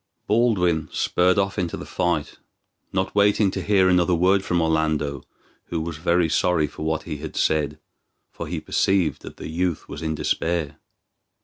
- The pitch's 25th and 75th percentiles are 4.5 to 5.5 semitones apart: No, average, 3.0 semitones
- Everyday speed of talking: Yes, average, 170 wpm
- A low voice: Yes, very low, 85 Hz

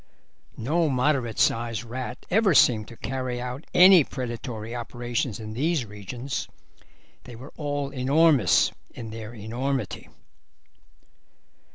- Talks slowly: Yes, slow, 110 wpm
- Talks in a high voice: No, low, 125 Hz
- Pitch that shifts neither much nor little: Yes, average, 3.3 semitones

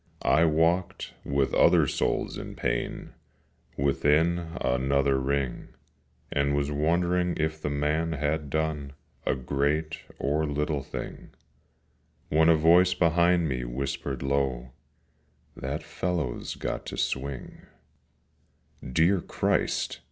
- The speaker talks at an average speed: No, slow, 110 wpm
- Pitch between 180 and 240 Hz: No, very low, 75 Hz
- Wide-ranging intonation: No, average, 2.9 semitones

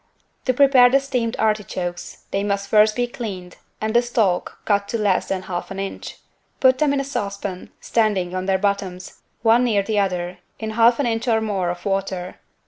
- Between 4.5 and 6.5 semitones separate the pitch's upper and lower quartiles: No, average, 3.7 semitones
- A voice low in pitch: No, high, 205 Hz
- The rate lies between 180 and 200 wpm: Yes, average, 195 wpm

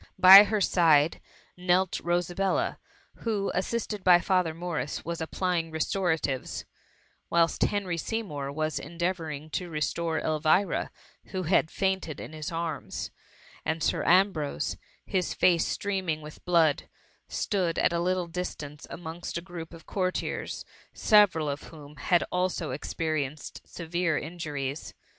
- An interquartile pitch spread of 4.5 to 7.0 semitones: No, average, 2.8 semitones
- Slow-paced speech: Yes, slow, 130 wpm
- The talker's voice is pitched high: No, medium, 170 Hz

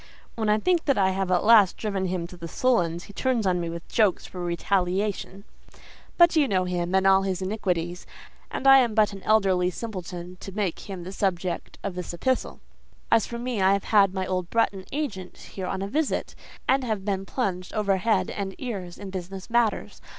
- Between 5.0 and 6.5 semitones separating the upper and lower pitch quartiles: No, average, 3.1 semitones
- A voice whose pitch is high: Yes, high, 195 Hz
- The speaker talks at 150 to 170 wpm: No, average, 200 wpm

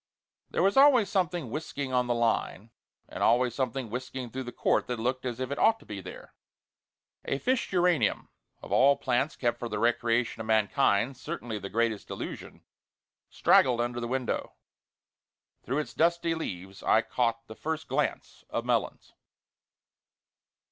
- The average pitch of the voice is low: Yes, low, 125 Hz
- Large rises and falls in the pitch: No, average, 3.6 semitones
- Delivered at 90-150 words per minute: No, average, 160 wpm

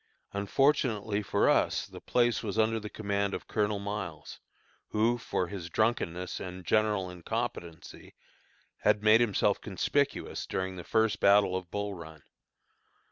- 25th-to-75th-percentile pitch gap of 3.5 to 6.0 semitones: No, average, 2.9 semitones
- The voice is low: Yes, low, 100 Hz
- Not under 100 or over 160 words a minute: Yes, slow, 135 wpm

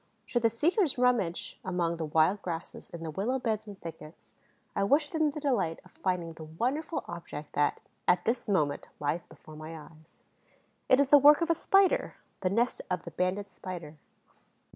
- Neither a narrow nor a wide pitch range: No, wide, 7.6 semitones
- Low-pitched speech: No, high, 190 Hz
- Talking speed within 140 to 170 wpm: No, average, 185 wpm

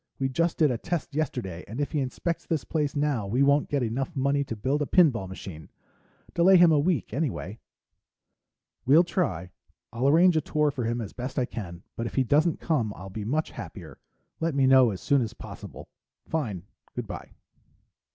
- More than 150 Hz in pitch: No, low, 135 Hz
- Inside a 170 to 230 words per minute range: Yes, average, 195 wpm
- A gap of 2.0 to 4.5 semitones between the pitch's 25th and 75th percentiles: No, average, 5.3 semitones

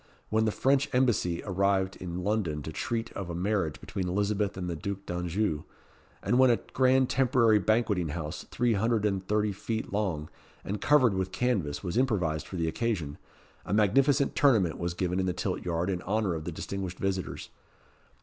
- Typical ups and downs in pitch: Yes, average, 4.2 semitones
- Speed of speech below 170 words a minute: No, average, 180 wpm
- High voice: No, low, 100 Hz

